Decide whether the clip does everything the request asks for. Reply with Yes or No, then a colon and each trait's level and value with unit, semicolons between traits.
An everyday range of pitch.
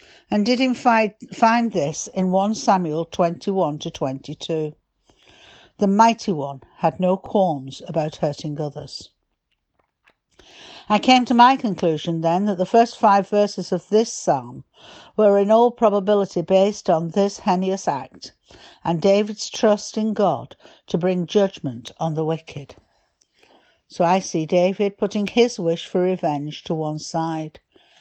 Yes: average, 4.4 semitones